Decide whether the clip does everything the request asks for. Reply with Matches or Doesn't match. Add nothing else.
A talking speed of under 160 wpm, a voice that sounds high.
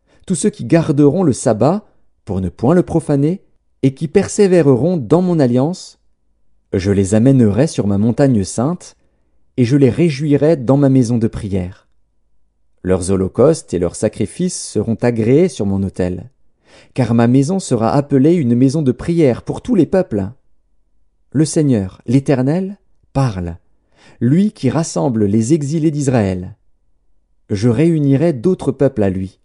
Doesn't match